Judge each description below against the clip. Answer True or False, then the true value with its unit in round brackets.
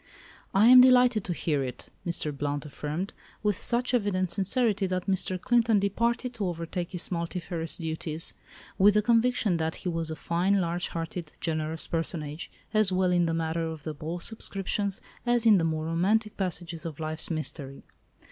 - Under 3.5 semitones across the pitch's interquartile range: False (4.2 semitones)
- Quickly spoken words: False (165 wpm)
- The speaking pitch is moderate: True (175 Hz)